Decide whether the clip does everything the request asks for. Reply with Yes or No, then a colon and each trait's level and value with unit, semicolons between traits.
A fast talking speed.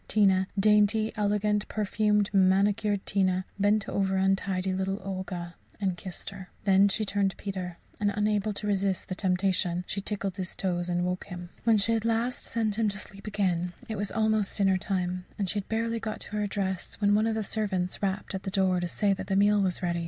Yes: fast, 210 wpm